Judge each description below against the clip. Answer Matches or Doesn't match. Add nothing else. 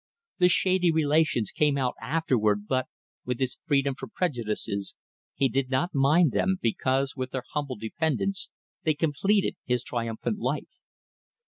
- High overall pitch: Doesn't match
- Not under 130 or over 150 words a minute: Matches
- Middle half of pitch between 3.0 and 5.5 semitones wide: Matches